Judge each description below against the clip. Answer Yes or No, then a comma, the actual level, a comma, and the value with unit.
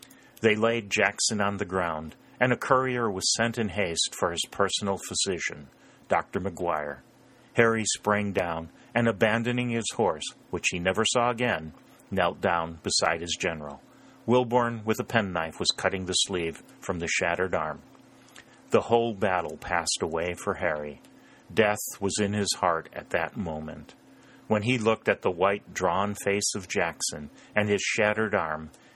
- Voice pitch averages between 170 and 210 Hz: No, low, 105 Hz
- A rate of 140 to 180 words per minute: Yes, average, 160 wpm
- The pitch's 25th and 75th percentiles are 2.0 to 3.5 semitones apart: No, average, 4.5 semitones